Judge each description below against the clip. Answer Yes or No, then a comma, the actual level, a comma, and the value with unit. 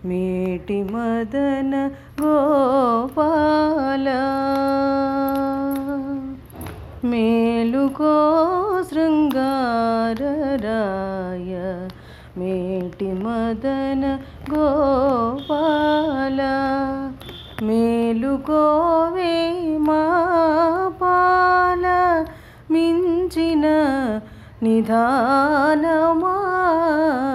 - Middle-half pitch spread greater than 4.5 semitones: Yes, average, 5.2 semitones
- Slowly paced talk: Yes, slow, 30 wpm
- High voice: Yes, very high, 275 Hz